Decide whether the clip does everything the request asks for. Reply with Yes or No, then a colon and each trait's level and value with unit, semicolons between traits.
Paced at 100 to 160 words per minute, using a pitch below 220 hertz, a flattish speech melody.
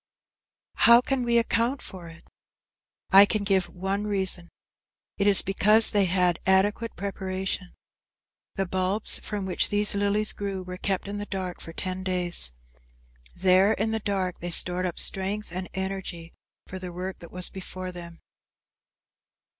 Yes: average, 155 wpm; high, 190 Hz; narrow, 2.0 semitones